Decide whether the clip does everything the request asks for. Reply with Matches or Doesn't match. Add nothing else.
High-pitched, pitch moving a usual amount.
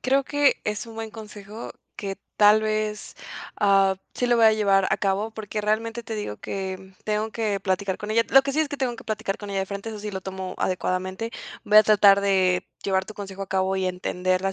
Doesn't match